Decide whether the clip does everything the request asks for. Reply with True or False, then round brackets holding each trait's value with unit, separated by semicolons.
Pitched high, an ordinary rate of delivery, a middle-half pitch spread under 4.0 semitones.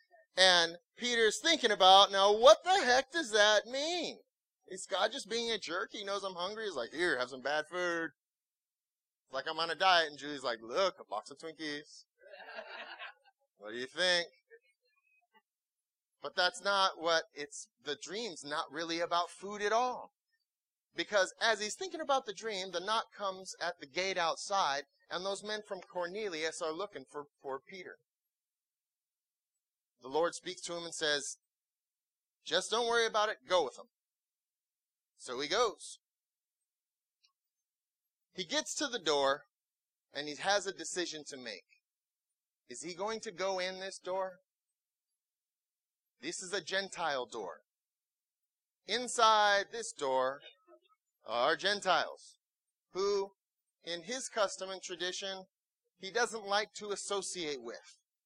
False (195 Hz; 145 wpm; 4.9 semitones)